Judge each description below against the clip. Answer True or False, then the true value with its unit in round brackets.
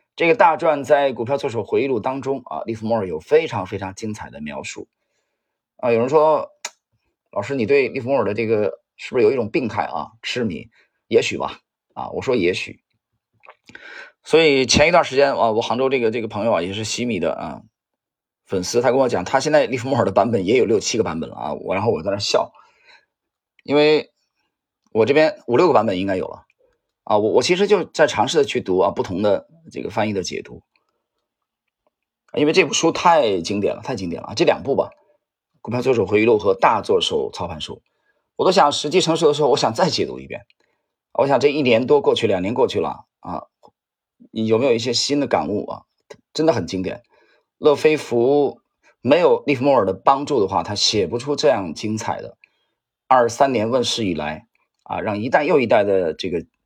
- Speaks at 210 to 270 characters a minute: False (290 characters per minute)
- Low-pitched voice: False (150 Hz)